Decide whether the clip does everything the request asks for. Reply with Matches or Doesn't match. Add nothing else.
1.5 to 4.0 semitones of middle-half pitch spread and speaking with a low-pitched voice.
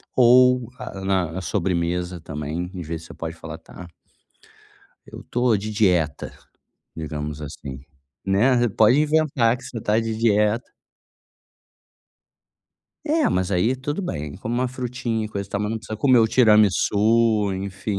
Doesn't match